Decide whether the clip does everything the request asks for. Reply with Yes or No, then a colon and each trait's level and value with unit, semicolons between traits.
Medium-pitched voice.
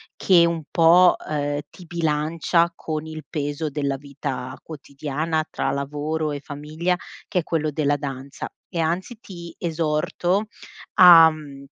Yes: medium, 155 Hz